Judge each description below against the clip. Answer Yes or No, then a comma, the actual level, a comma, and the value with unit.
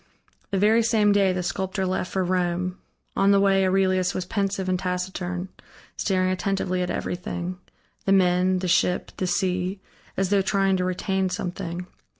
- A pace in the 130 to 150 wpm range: No, average, 160 wpm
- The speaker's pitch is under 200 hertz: Yes, medium, 185 Hz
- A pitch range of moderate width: No, narrow, 1.2 semitones